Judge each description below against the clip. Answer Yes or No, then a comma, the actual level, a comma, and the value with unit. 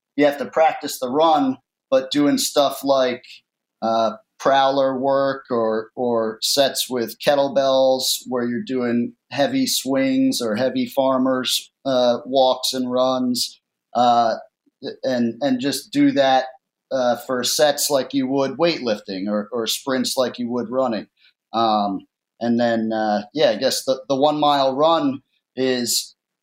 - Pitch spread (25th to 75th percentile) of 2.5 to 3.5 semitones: Yes, average, 3.0 semitones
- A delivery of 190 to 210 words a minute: No, average, 145 wpm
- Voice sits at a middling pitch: No, low, 130 Hz